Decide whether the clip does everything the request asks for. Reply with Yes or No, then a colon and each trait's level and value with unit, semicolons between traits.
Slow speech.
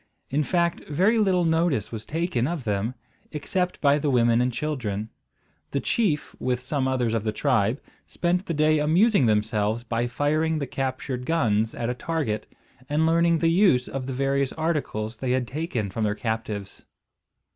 No: average, 170 wpm